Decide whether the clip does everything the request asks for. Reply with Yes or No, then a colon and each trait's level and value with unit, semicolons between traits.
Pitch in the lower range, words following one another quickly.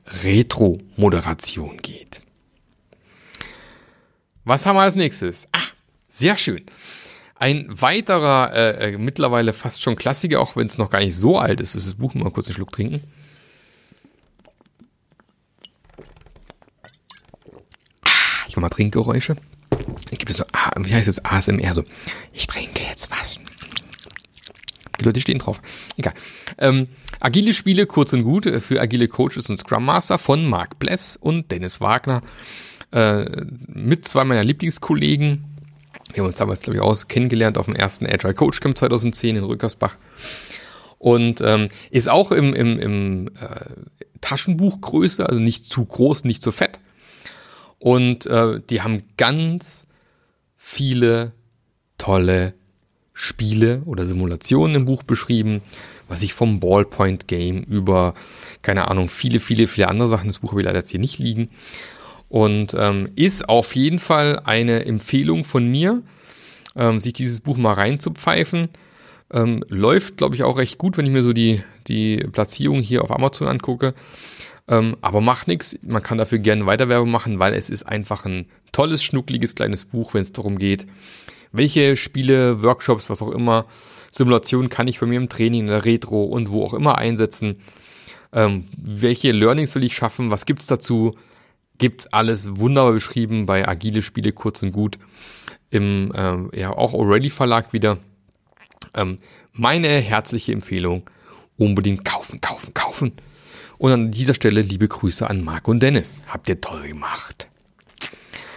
No: low, 115 Hz; average, 150 wpm